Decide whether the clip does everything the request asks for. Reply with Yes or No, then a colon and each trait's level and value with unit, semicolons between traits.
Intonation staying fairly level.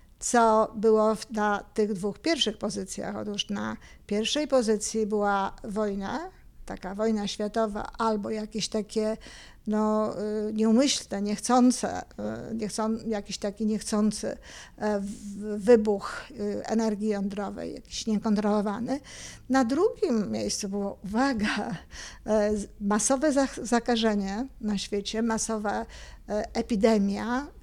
Yes: narrow, 1.5 semitones